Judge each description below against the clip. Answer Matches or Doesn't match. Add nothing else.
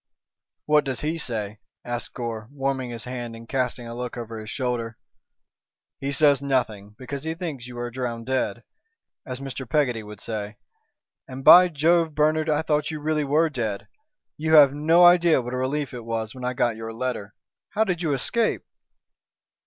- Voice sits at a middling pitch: Doesn't match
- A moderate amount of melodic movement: Matches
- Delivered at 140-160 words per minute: Doesn't match